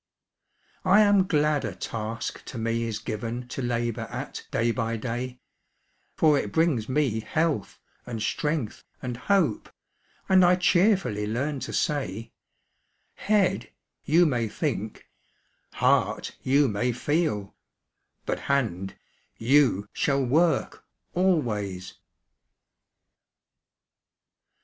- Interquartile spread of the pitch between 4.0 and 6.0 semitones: Yes, wide, 5.5 semitones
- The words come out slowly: Yes, slow, 105 wpm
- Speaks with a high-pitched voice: No, low, 125 Hz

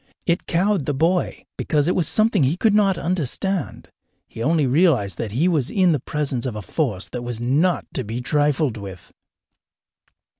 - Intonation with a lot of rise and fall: Yes, wide, 6.4 semitones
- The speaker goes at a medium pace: Yes, average, 180 wpm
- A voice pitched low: No, medium, 150 Hz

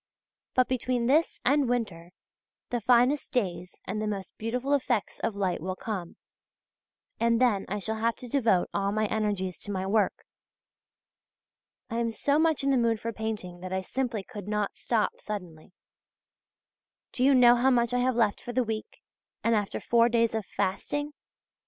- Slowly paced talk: No, average, 175 wpm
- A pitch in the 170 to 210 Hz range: No, high, 225 Hz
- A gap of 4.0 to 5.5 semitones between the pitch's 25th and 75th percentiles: No, average, 3.5 semitones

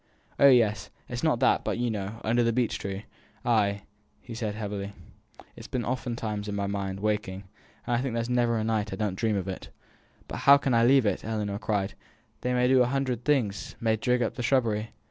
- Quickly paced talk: Yes, fast, 225 wpm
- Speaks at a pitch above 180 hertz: No, low, 110 Hz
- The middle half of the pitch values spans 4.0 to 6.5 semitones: No, average, 3.0 semitones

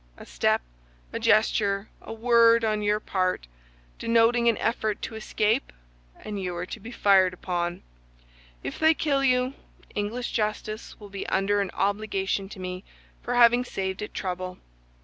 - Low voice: No, high, 210 Hz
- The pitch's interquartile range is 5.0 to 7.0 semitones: No, average, 3.3 semitones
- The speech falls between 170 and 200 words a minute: No, average, 155 wpm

